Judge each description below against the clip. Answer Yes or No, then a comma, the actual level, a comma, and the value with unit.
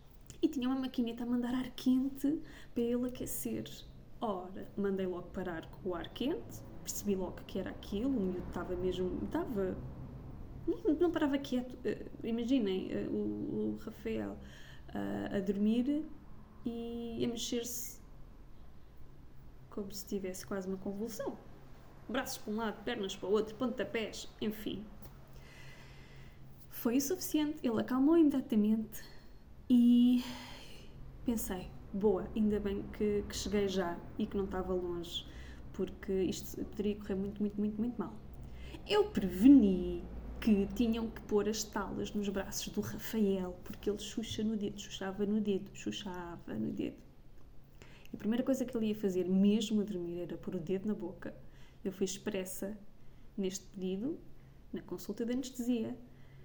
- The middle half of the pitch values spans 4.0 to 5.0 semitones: Yes, average, 4.4 semitones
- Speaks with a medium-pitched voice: No, high, 210 Hz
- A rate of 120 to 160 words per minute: Yes, average, 140 wpm